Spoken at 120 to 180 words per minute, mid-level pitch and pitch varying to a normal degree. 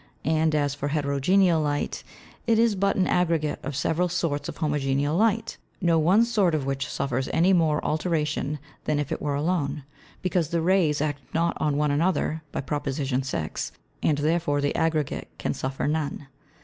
Yes: average, 175 wpm; medium, 155 Hz; average, 3.1 semitones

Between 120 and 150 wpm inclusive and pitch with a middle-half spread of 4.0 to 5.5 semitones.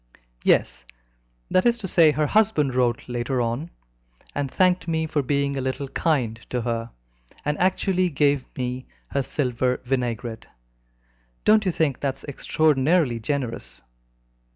Yes: average, 140 wpm; average, 4.4 semitones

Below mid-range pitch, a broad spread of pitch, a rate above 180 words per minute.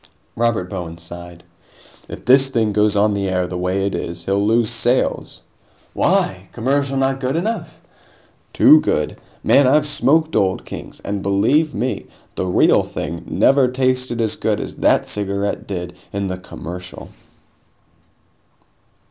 No: low, 105 Hz; wide, 5.9 semitones; average, 145 wpm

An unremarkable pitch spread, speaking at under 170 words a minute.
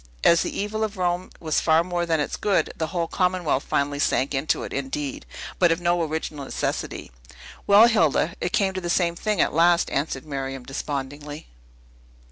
No: average, 3.9 semitones; average, 180 wpm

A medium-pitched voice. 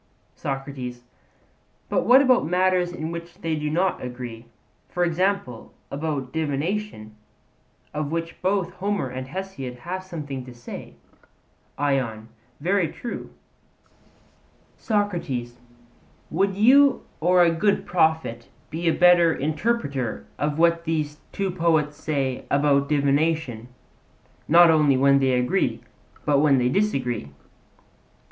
Yes: medium, 155 Hz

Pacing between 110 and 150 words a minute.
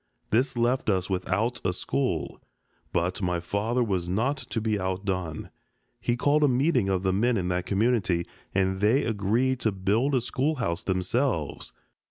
No: average, 160 wpm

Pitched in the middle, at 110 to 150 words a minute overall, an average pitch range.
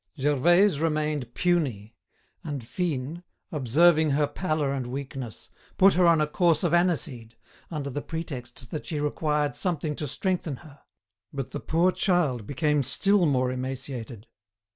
Yes: medium, 150 Hz; average, 140 wpm; average, 4.3 semitones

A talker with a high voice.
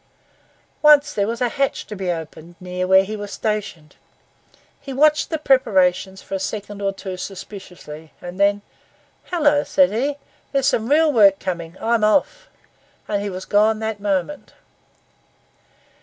Yes: high, 205 Hz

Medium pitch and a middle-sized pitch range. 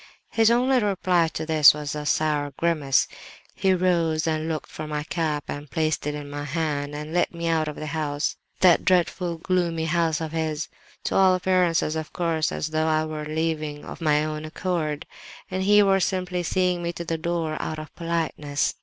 No: medium, 160 Hz; narrow, 2.3 semitones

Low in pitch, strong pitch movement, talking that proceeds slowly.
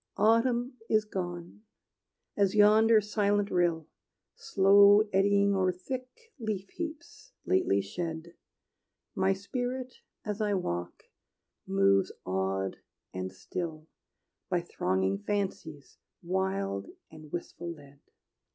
No: high, 190 Hz; wide, 5.8 semitones; slow, 100 wpm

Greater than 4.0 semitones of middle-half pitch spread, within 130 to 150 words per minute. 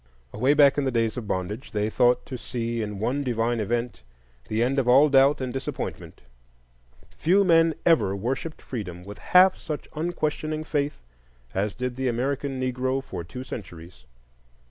No: average, 4.4 semitones; average, 165 wpm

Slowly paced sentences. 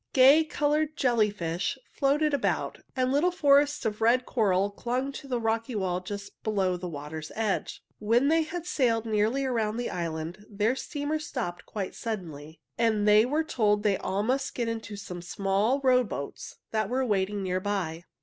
No: average, 170 wpm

